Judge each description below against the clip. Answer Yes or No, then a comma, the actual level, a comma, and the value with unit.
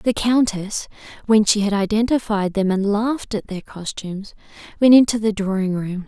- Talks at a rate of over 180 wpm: No, average, 170 wpm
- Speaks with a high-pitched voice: Yes, high, 210 Hz